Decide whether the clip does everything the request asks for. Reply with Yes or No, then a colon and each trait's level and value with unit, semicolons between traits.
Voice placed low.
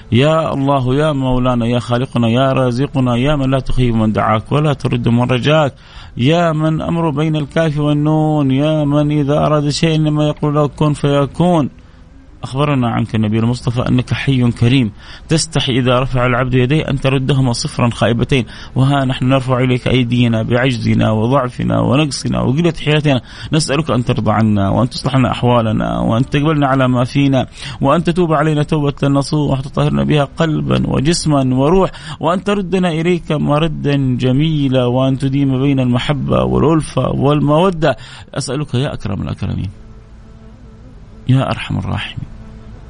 Yes: low, 130 Hz